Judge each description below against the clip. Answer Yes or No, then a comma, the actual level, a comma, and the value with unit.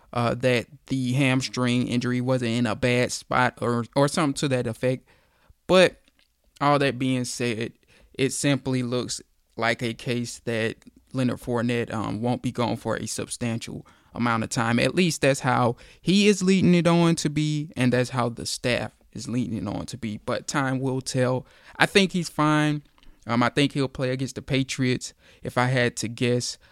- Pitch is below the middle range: Yes, low, 125 Hz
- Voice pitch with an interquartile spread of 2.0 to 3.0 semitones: Yes, narrow, 2.4 semitones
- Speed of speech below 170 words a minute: No, average, 185 wpm